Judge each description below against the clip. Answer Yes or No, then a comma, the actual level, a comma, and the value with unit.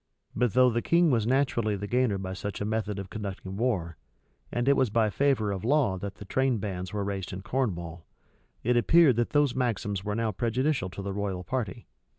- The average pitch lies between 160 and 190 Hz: No, low, 110 Hz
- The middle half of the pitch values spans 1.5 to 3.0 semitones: No, average, 4.4 semitones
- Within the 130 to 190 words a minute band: No, fast, 205 wpm